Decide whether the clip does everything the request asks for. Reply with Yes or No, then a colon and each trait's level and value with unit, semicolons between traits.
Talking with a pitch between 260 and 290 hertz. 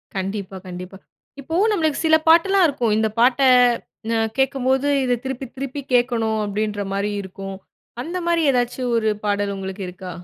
No: high, 240 Hz